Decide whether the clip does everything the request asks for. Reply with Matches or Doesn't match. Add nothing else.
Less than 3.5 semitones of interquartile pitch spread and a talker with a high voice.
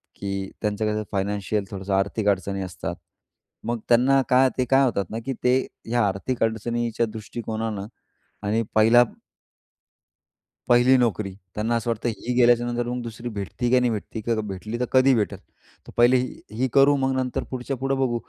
Doesn't match